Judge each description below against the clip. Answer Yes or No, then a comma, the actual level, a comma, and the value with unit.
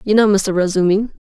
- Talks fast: No, average, 195 wpm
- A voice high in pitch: Yes, high, 200 Hz